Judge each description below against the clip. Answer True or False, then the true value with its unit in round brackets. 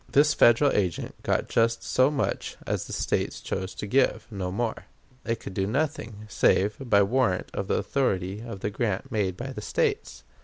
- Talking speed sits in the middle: True (185 wpm)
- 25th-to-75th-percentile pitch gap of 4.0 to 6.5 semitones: True (5.0 semitones)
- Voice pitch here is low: True (110 Hz)